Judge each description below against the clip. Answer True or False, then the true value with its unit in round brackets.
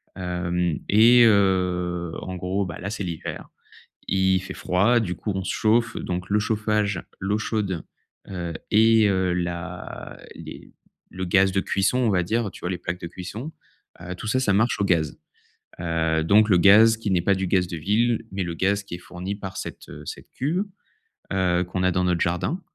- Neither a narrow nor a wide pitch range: True (3.1 semitones)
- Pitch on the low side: True (95 Hz)